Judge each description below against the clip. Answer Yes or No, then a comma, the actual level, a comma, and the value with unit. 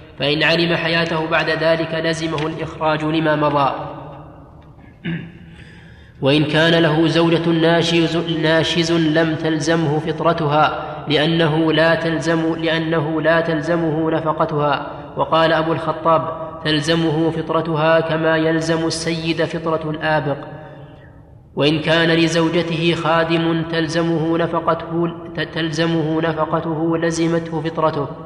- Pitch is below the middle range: No, medium, 160 Hz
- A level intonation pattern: Yes, narrow, 0.9 semitones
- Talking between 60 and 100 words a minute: Yes, average, 95 wpm